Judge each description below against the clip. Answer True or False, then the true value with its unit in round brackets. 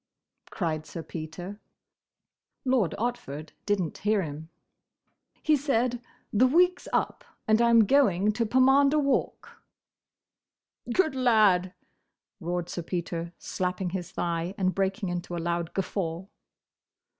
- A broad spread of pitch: True (5.9 semitones)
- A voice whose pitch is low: False (195 Hz)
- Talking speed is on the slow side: True (120 wpm)